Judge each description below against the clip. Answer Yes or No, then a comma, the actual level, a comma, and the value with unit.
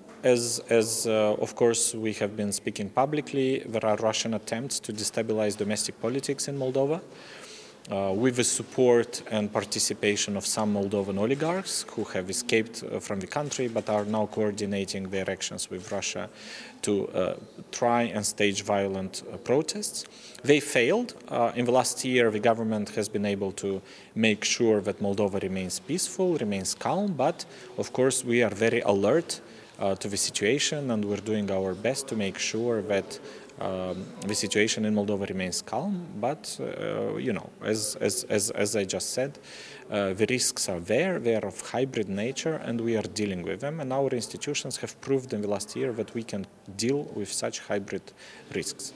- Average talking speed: Yes, average, 175 wpm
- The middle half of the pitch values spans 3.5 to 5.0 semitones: Yes, average, 3.8 semitones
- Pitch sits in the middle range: No, low, 110 Hz